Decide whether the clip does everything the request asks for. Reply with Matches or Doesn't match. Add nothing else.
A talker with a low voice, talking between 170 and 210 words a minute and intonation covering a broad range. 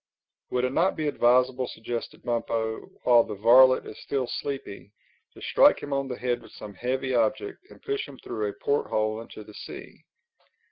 Doesn't match